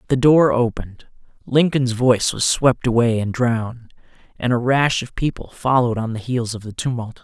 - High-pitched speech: No, low, 120 Hz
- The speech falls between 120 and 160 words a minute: No, average, 180 wpm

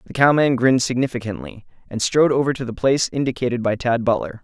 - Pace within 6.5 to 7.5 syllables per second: Yes, 6.7 syllables/s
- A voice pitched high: No, low, 125 Hz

